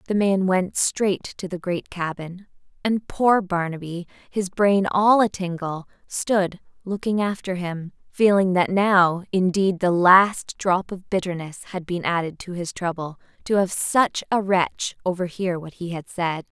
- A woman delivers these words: Yes, female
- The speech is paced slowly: No, average, 160 wpm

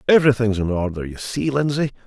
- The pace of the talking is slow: No, fast, 205 wpm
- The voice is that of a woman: No, male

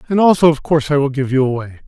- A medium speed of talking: No, fast, 290 wpm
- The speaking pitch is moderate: Yes, medium, 145 Hz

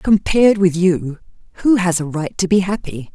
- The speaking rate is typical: Yes, average, 190 wpm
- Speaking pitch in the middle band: Yes, medium, 180 Hz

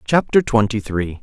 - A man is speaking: Yes, male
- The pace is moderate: Yes, average, 145 wpm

